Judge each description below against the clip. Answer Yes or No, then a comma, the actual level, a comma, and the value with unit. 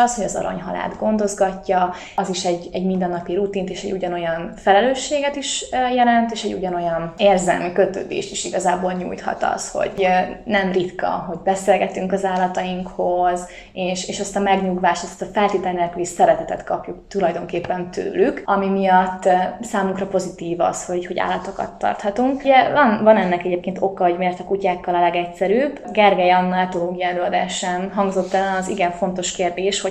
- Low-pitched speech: No, medium, 185 Hz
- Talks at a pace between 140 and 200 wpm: Yes, fast, 155 wpm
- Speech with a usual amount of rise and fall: No, narrow, 1.9 semitones